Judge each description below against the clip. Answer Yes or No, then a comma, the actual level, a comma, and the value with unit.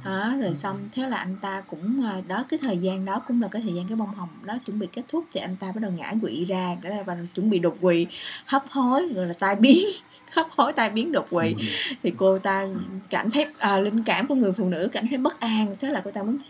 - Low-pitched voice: No, high, 205 Hz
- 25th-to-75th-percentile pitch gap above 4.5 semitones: Yes, average, 5.0 semitones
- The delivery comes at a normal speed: No, fast, 260 wpm